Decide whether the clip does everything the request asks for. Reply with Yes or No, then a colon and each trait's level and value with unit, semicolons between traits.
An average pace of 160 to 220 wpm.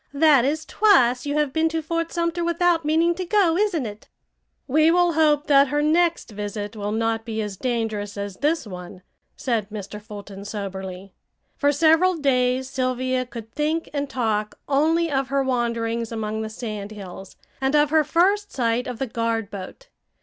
Yes: average, 175 wpm